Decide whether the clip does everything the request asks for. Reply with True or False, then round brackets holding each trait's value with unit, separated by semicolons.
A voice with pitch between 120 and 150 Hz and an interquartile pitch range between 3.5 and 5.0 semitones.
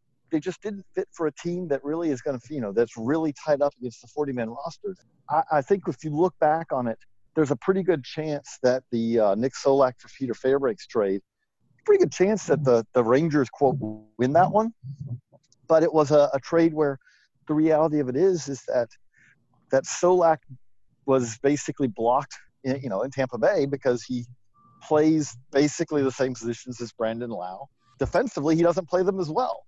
True (140 Hz; 4.4 semitones)